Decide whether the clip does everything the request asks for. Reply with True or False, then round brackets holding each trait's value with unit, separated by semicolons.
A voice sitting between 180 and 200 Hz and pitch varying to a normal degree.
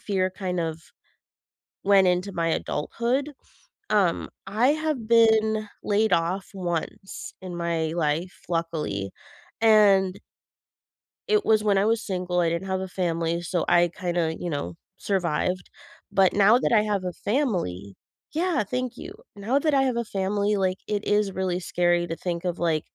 True (190 Hz; 3.7 semitones)